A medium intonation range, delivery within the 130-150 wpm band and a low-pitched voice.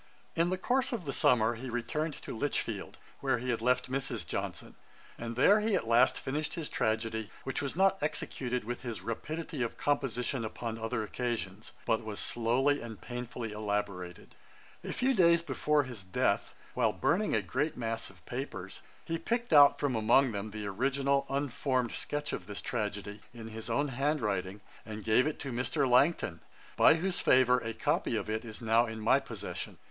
No: average, 4.6 semitones; average, 185 wpm; low, 125 Hz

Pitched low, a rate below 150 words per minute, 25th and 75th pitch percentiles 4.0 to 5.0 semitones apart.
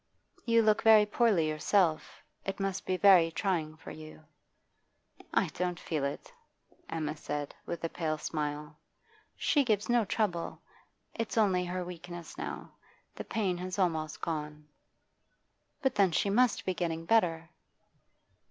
No: medium, 175 Hz; average, 140 wpm; average, 4.4 semitones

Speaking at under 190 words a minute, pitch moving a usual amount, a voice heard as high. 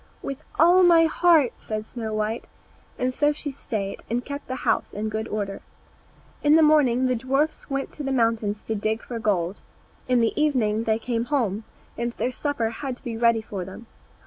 No: average, 195 wpm; average, 4.5 semitones; high, 235 Hz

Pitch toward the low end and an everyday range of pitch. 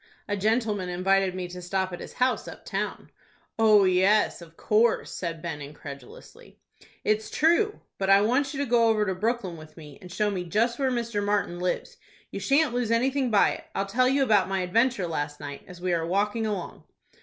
No: high, 205 Hz; average, 4.6 semitones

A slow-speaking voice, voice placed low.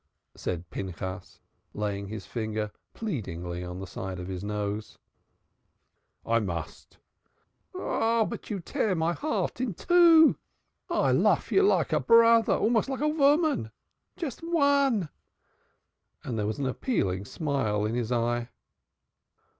Yes: slow, 120 wpm; low, 120 Hz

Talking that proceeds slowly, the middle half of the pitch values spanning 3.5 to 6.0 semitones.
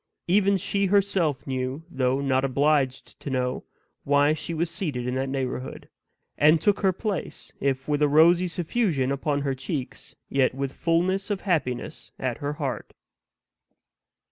No: average, 150 wpm; average, 4.9 semitones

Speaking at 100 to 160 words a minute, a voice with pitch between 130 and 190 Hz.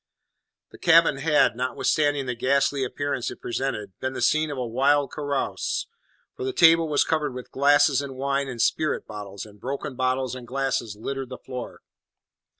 No: average, 170 wpm; low, 135 Hz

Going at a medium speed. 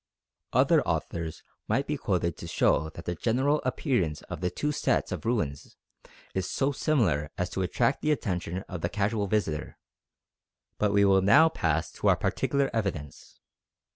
Yes: average, 165 wpm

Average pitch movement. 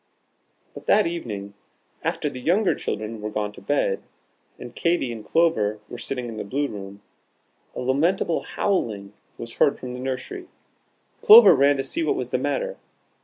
No: wide, 7.8 semitones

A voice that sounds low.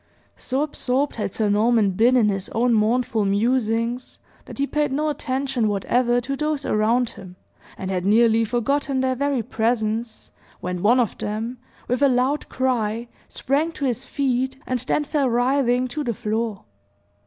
No: high, 245 Hz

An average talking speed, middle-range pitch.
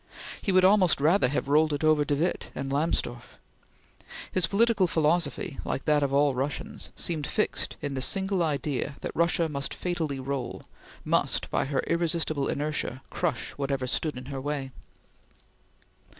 Yes: average, 155 wpm; medium, 150 Hz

